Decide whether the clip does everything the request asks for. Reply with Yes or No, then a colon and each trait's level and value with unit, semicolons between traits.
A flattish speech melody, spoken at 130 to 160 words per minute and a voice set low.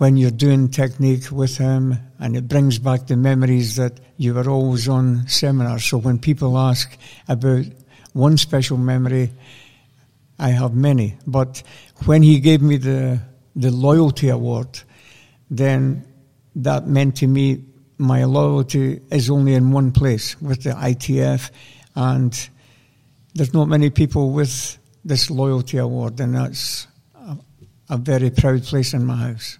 Yes: narrow, 1.4 semitones; average, 145 wpm; low, 130 Hz